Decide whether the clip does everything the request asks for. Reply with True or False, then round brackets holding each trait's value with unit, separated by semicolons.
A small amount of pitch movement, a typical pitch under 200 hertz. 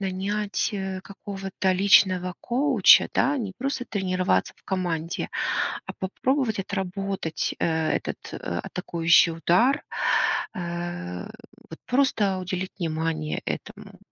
False (3.0 semitones; 190 Hz)